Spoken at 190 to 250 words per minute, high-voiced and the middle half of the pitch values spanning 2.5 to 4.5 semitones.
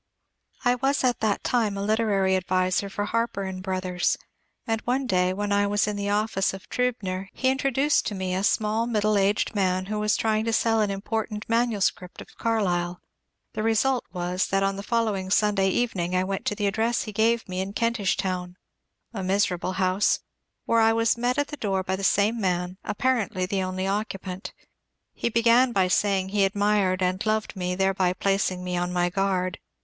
Yes: average, 195 wpm; high, 200 Hz; average, 3.1 semitones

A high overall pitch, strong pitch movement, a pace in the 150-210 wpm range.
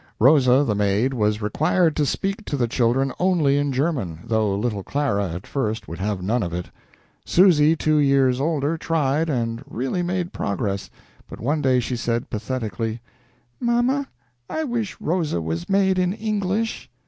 No: low, 135 Hz; wide, 7.1 semitones; average, 160 wpm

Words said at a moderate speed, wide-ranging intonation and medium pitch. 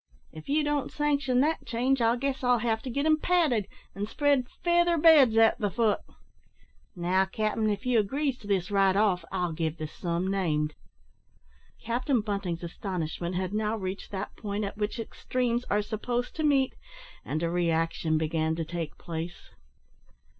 No: average, 170 wpm; wide, 6.1 semitones; high, 210 Hz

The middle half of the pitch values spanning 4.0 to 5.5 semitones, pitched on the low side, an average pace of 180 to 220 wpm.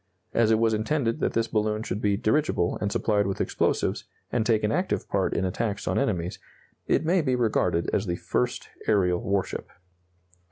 No: average, 2.8 semitones; low, 110 Hz; average, 185 wpm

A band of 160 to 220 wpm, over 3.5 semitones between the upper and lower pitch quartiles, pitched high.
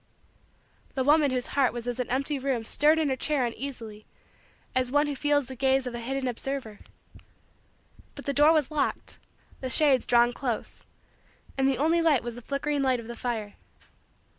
No: average, 185 wpm; average, 2.9 semitones; very high, 265 Hz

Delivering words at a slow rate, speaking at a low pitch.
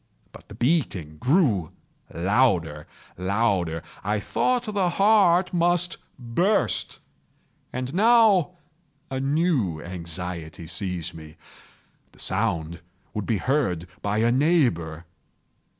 Yes: slow, 100 wpm; low, 115 Hz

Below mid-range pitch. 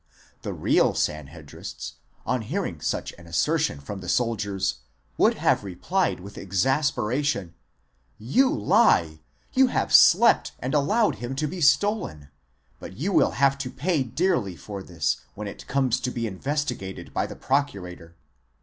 Yes: low, 120 Hz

